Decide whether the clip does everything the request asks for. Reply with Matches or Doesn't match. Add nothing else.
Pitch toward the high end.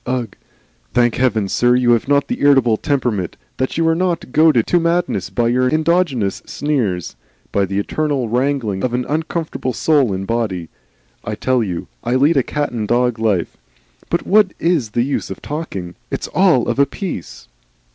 Doesn't match